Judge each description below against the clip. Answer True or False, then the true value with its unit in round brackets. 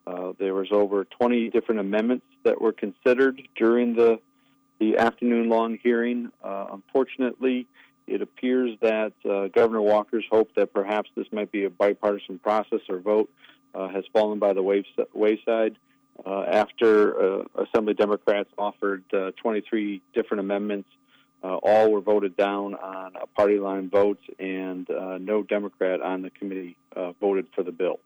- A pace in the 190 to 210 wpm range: False (160 wpm)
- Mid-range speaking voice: False (105 Hz)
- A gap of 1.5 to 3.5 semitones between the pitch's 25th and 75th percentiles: True (2.9 semitones)